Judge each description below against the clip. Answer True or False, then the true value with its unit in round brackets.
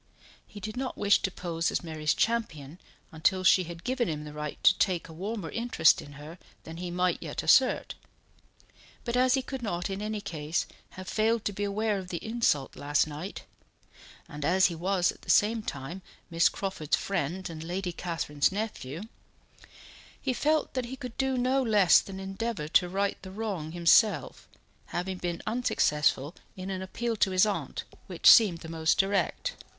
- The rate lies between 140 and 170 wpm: False (180 wpm)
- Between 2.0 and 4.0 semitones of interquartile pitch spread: False (4.7 semitones)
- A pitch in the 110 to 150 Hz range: False (190 Hz)